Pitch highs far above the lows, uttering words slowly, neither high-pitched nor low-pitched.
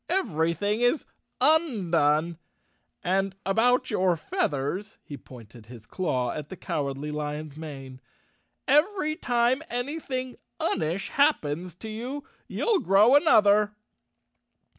No: wide, 8.7 semitones; slow, 110 wpm; high, 195 Hz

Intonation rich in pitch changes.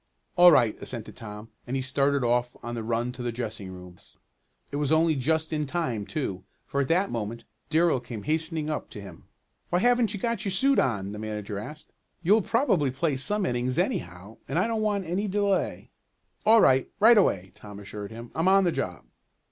Yes: wide, 8.0 semitones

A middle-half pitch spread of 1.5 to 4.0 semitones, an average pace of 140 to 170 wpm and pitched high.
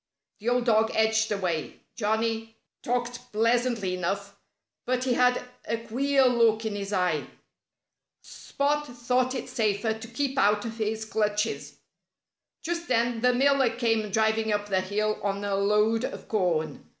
Yes: average, 2.9 semitones; average, 150 wpm; high, 225 Hz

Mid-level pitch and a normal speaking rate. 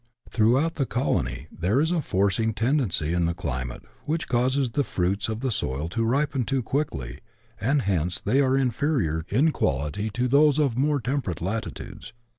No: low, 115 Hz; average, 170 wpm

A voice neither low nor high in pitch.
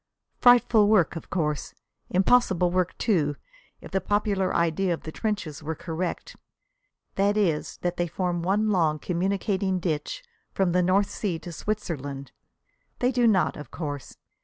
Yes: medium, 180 Hz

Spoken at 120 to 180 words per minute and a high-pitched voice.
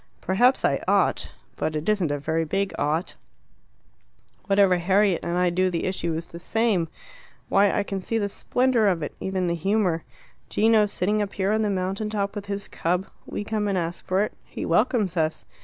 No: average, 195 wpm; high, 195 Hz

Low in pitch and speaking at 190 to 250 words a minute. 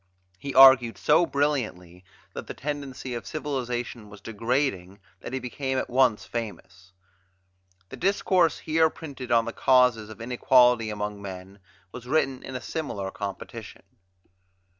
No: low, 125 Hz; average, 140 wpm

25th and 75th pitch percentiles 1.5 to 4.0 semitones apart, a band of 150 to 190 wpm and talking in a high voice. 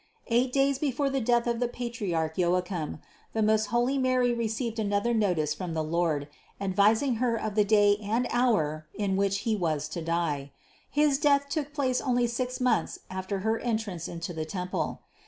No: wide, 5.6 semitones; average, 175 wpm; high, 215 Hz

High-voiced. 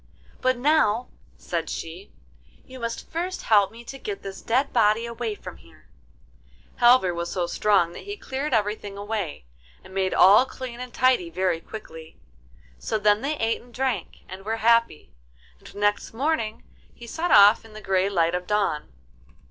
Yes: high, 215 Hz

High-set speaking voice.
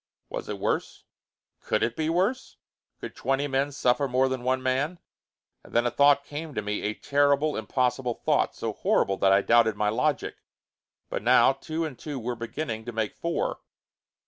No: low, 130 Hz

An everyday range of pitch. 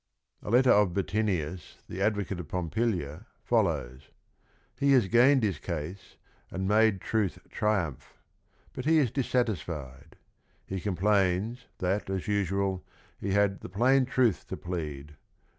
Yes: average, 4.2 semitones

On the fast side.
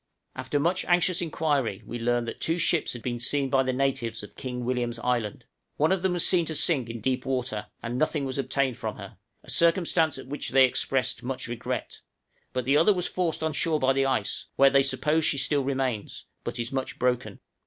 Yes: fast, 215 wpm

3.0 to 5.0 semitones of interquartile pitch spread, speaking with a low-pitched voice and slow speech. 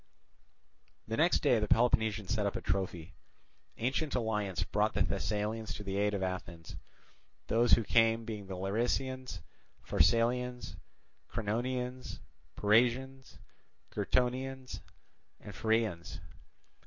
Yes: average, 3.5 semitones; low, 110 Hz; slow, 110 wpm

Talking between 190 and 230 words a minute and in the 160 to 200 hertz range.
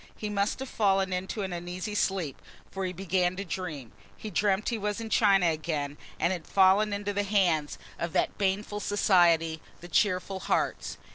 No: average, 180 wpm; high, 190 Hz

